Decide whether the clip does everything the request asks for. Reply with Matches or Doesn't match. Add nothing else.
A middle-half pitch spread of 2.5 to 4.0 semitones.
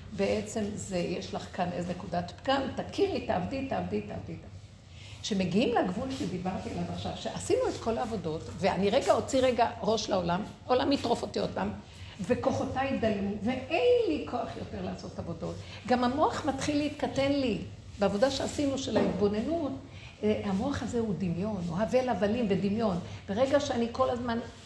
Doesn't match